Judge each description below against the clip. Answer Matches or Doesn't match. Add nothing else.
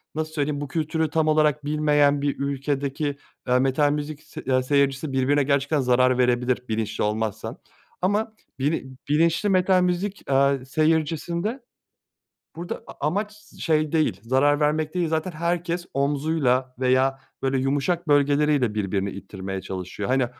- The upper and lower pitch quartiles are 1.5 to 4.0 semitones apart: Matches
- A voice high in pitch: Doesn't match